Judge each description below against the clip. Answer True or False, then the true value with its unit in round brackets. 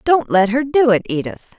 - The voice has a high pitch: True (230 Hz)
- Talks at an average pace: False (225 wpm)